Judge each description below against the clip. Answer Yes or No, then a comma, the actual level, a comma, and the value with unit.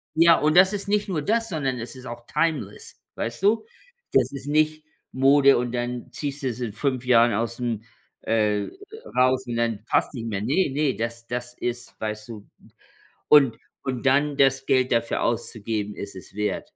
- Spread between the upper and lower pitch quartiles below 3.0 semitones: No, average, 3.8 semitones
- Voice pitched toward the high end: No, low, 125 Hz